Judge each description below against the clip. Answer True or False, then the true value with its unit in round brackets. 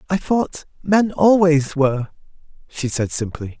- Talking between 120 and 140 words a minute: True (135 wpm)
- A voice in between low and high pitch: True (155 Hz)